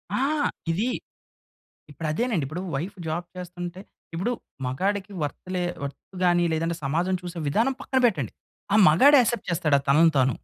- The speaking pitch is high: No, medium, 175 Hz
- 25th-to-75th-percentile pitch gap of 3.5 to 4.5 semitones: Yes, average, 4.0 semitones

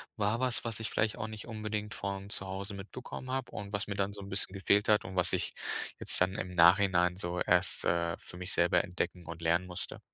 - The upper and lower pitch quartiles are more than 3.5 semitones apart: No, average, 2.9 semitones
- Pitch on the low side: Yes, low, 100 Hz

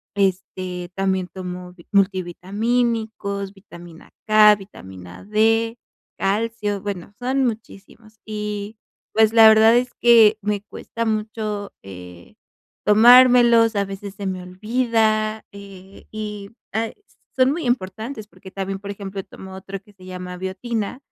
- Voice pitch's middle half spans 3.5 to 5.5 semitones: No, average, 2.8 semitones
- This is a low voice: No, high, 205 Hz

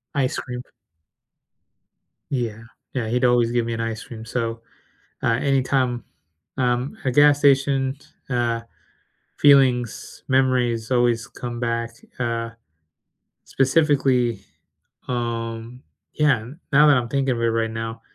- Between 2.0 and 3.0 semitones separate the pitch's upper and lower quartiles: Yes, narrow, 2.4 semitones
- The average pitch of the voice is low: Yes, low, 120 Hz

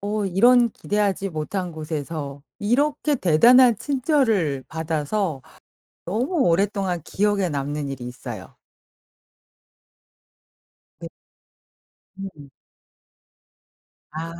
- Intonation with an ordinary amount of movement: No, wide, 5.9 semitones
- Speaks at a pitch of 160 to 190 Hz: Yes, medium, 185 Hz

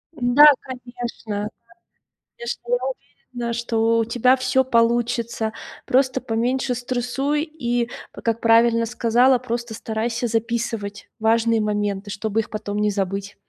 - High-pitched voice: Yes, high, 235 Hz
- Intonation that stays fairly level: Yes, narrow, 1.9 semitones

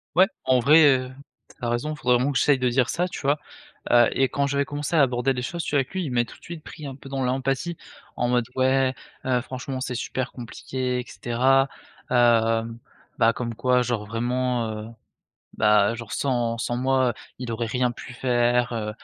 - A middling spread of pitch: No, narrow, 2.0 semitones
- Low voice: Yes, low, 125 Hz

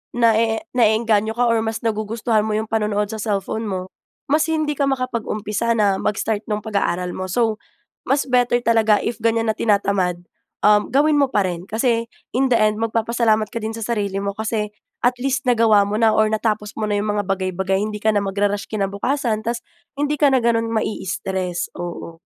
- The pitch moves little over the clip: Yes, narrow, 2.2 semitones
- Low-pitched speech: No, high, 220 Hz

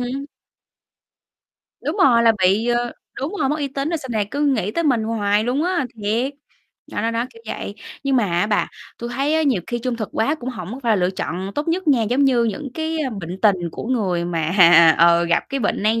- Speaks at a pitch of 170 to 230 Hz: No, high, 240 Hz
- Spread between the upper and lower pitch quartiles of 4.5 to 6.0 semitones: Yes, average, 5.0 semitones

